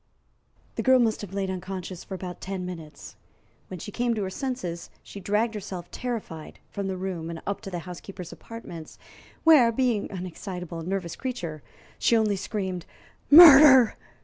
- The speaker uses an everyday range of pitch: Yes, average, 4.4 semitones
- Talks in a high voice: Yes, high, 195 Hz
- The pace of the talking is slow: No, average, 170 wpm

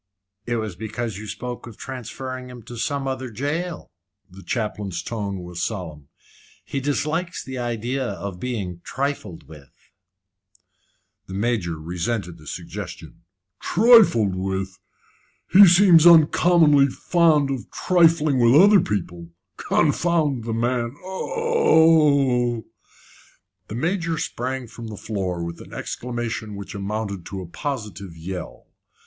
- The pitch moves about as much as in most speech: No, wide, 6.8 semitones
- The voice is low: Yes, low, 120 Hz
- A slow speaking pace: Yes, slow, 125 wpm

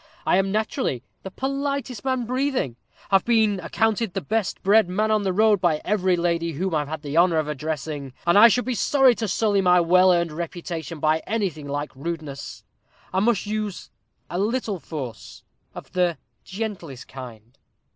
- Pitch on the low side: No, medium, 185 Hz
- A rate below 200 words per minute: Yes, average, 175 wpm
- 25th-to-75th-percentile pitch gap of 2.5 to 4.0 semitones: No, wide, 5.5 semitones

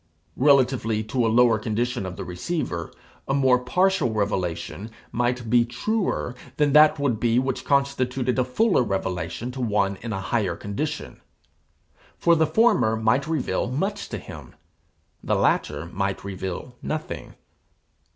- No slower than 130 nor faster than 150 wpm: Yes, average, 140 wpm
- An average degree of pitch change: Yes, average, 5.0 semitones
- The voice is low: Yes, low, 120 Hz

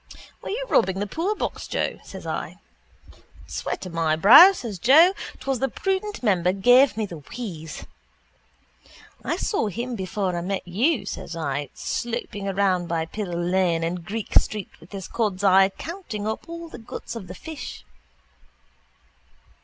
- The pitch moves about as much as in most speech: No, wide, 5.8 semitones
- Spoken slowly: No, average, 155 wpm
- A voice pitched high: Yes, high, 200 Hz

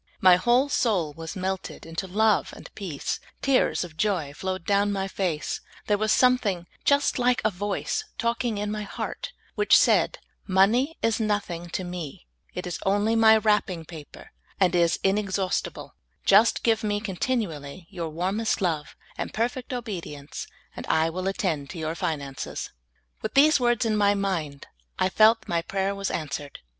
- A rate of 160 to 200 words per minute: Yes, average, 170 wpm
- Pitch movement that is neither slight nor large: Yes, average, 4.3 semitones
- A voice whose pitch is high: Yes, high, 195 Hz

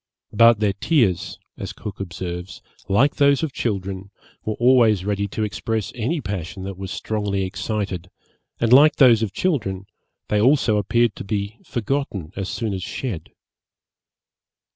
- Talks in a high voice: No, low, 105 Hz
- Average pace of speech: Yes, average, 145 wpm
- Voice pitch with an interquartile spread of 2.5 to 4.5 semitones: Yes, average, 3.6 semitones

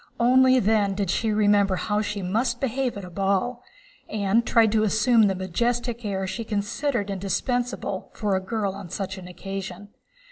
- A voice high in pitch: Yes, high, 205 Hz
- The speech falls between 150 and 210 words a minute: Yes, average, 170 wpm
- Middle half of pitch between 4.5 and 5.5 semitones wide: No, average, 3.4 semitones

